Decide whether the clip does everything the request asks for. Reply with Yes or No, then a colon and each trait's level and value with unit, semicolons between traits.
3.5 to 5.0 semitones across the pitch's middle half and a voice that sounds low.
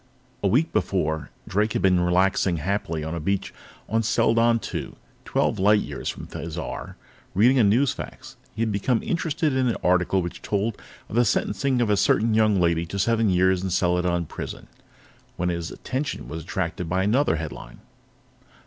Yes: average, 4.5 semitones; very low, 95 Hz